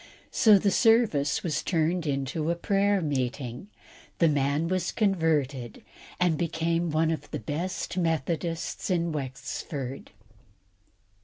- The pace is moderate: No, slow, 115 wpm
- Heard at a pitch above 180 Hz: No, medium, 160 Hz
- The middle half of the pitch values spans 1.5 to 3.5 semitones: No, average, 3.9 semitones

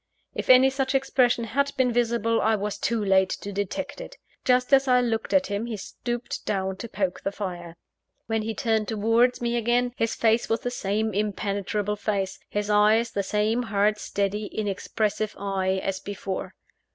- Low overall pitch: No, high, 215 Hz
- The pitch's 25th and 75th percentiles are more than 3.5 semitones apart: No, average, 2.9 semitones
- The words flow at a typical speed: Yes, average, 175 wpm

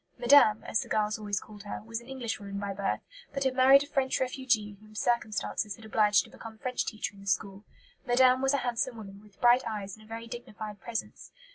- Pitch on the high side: Yes, high, 220 Hz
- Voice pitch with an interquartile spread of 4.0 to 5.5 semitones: No, average, 3.2 semitones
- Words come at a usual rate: No, fast, 220 wpm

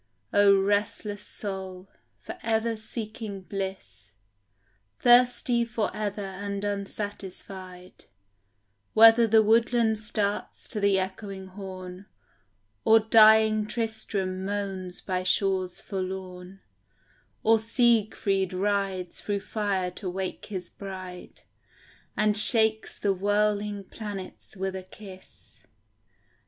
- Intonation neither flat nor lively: No, narrow, 2.3 semitones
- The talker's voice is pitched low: No, high, 200 Hz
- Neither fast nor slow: No, slow, 100 wpm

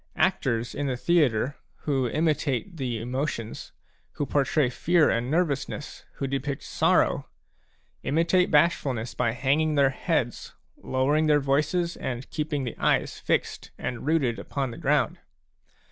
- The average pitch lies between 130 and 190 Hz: Yes, medium, 140 Hz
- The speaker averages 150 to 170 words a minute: No, slow, 135 wpm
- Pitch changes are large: No, average, 3.4 semitones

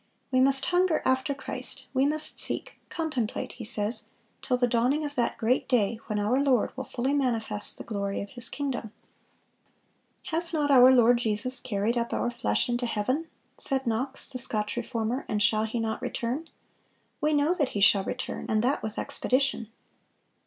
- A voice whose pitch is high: Yes, high, 245 Hz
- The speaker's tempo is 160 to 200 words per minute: Yes, average, 175 wpm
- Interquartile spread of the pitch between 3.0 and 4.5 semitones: Yes, average, 3.7 semitones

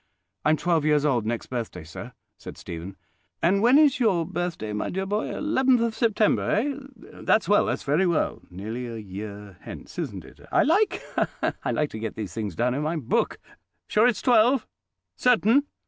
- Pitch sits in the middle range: Yes, medium, 165 Hz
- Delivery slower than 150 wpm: No, average, 180 wpm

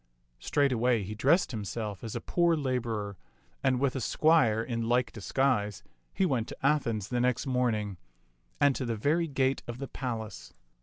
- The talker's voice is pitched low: Yes, low, 125 Hz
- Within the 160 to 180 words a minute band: Yes, average, 165 wpm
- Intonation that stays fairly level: No, average, 3.7 semitones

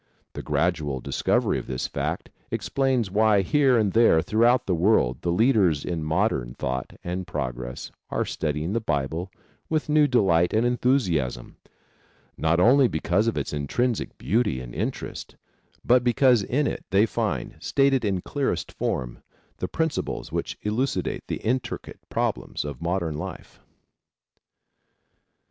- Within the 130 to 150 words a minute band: Yes, average, 140 wpm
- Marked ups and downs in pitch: Yes, wide, 7.8 semitones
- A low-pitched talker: Yes, very low, 95 Hz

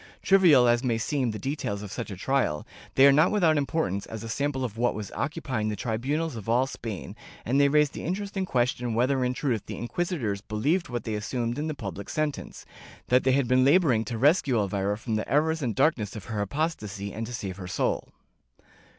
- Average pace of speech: No, fast, 210 wpm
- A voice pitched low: Yes, low, 125 Hz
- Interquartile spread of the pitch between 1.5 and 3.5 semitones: No, average, 5.2 semitones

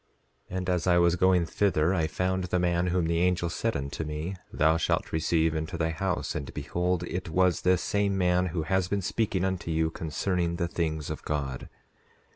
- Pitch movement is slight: Yes, narrow, 2.2 semitones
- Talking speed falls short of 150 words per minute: No, average, 190 wpm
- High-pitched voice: No, very low, 85 Hz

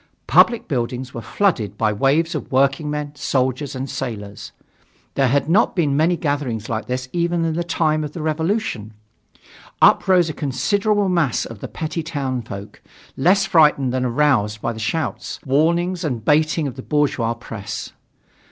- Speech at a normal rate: Yes, average, 160 wpm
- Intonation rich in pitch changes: No, average, 4.9 semitones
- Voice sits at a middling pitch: Yes, medium, 145 Hz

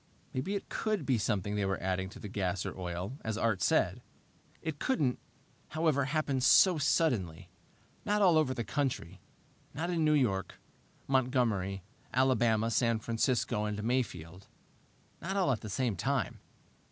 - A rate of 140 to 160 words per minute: Yes, average, 155 wpm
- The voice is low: Yes, low, 120 Hz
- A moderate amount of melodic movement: No, wide, 6.2 semitones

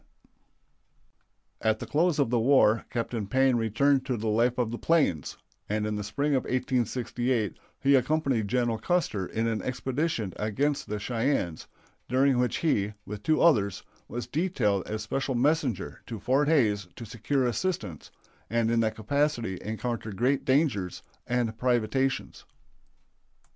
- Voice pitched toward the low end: Yes, low, 120 Hz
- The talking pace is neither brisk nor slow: Yes, average, 150 wpm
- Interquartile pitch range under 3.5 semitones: No, average, 4.1 semitones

